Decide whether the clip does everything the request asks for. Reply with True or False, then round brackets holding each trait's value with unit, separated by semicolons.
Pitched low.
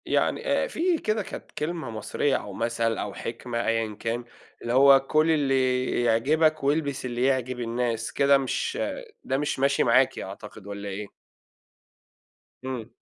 True (125 Hz)